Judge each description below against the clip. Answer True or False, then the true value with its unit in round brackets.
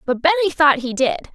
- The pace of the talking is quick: True (225 wpm)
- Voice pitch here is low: False (295 Hz)